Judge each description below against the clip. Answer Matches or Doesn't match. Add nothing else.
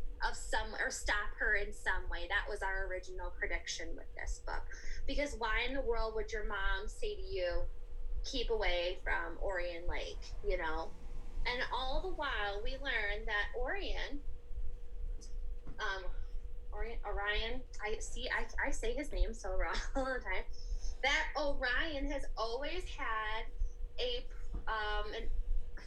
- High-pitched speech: Matches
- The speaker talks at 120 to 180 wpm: Matches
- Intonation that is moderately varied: Doesn't match